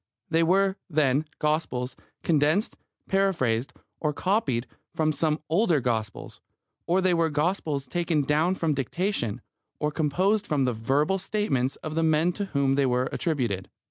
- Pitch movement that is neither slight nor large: Yes, average, 4.7 semitones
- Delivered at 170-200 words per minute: No, average, 145 wpm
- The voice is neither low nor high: Yes, medium, 155 Hz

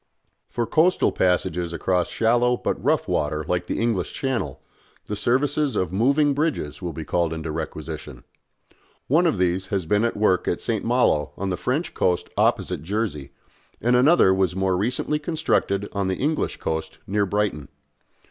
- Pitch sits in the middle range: No, low, 100 Hz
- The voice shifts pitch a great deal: Yes, wide, 5.8 semitones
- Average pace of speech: Yes, average, 165 wpm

